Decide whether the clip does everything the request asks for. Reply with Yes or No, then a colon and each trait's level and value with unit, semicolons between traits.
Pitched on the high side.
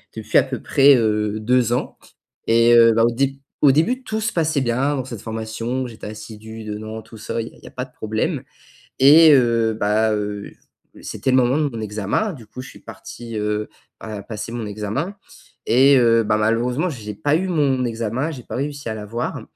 No: low, 115 Hz